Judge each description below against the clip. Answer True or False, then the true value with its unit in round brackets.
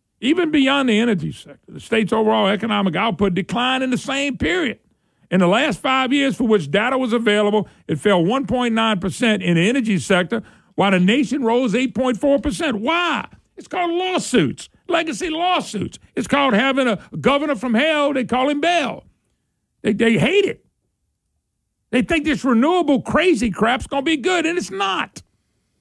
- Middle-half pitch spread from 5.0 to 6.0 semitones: True (5.3 semitones)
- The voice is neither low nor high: False (255 Hz)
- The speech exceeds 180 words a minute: False (165 wpm)